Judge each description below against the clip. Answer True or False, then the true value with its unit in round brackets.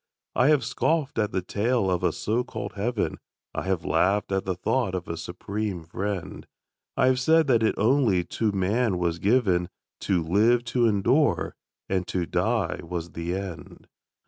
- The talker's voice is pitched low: True (100 Hz)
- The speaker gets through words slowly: False (170 wpm)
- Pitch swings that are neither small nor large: True (5.0 semitones)